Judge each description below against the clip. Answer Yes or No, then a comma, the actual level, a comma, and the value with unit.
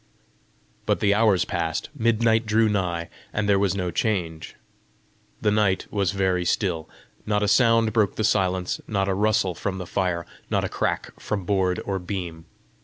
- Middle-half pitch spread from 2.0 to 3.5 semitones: Yes, average, 2.8 semitones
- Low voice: Yes, low, 100 Hz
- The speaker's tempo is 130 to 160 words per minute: No, average, 170 wpm